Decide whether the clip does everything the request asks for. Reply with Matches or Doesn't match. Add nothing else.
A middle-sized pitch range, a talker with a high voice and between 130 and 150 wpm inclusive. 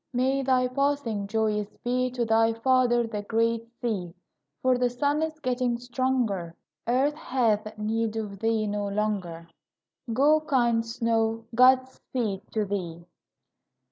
Matches